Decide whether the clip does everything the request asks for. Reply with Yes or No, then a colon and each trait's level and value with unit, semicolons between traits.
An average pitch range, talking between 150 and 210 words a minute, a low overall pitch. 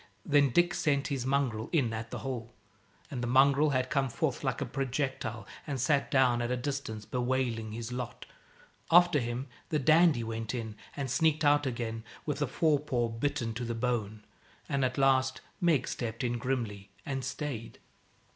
Yes: average, 3.3 semitones; average, 175 wpm; low, 130 Hz